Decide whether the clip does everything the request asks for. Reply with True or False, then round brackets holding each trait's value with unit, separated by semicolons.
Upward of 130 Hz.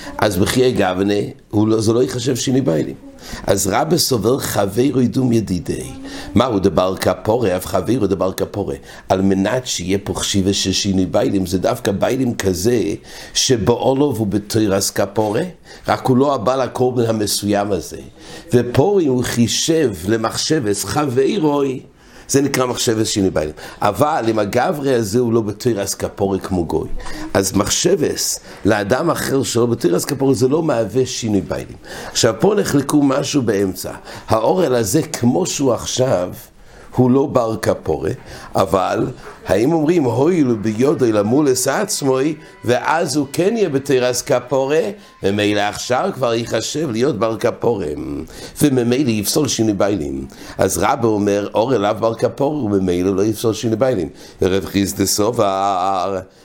False (115 Hz)